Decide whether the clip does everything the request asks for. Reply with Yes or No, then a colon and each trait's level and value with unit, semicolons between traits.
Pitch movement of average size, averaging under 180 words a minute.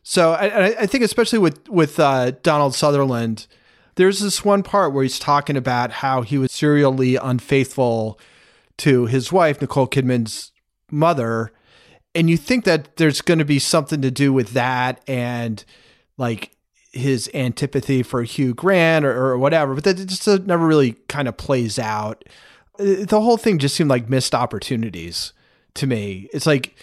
Yes: average, 4.6 semitones; average, 165 wpm